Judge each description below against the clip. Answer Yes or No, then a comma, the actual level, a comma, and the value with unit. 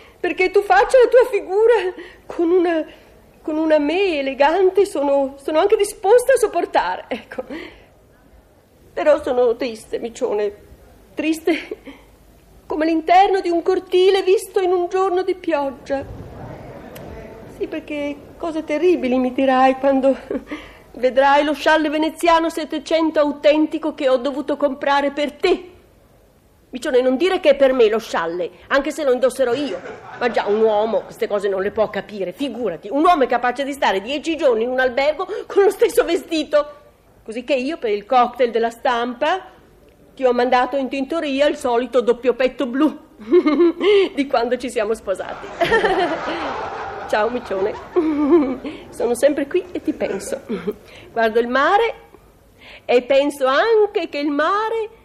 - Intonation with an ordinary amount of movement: No, wide, 5.7 semitones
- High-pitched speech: Yes, very high, 295 Hz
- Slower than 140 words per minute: No, average, 145 wpm